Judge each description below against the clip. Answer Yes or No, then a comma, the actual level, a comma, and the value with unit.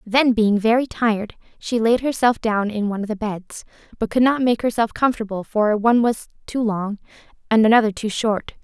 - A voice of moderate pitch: No, high, 225 Hz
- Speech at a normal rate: Yes, average, 195 wpm